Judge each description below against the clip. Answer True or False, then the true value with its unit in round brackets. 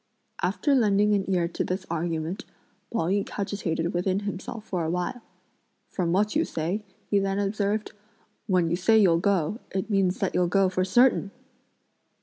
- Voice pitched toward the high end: True (195 Hz)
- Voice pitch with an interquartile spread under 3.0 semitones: True (2.6 semitones)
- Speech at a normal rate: True (165 wpm)